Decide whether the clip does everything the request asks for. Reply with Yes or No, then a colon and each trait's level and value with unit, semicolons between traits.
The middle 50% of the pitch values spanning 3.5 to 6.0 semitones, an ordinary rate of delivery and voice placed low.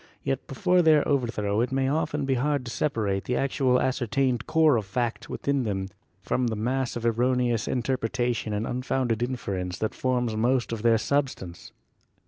No: average, 2.9 semitones; average, 170 wpm; low, 125 Hz